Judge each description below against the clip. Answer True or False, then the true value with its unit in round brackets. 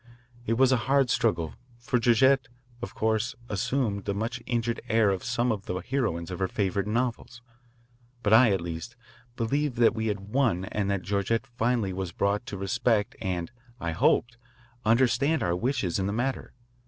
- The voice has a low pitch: True (110 Hz)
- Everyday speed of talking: True (175 wpm)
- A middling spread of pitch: True (3.8 semitones)